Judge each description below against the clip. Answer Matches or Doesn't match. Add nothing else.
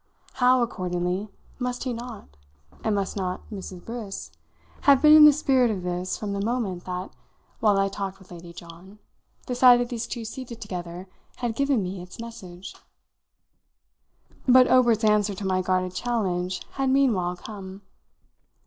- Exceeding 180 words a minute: Doesn't match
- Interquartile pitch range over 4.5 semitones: Matches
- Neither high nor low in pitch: Doesn't match